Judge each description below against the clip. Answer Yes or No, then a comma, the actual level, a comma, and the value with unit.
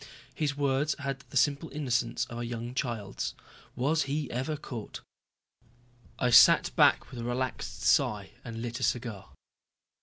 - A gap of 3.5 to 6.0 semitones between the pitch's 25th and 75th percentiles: No, average, 3.0 semitones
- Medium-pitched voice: No, low, 125 Hz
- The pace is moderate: Yes, average, 150 wpm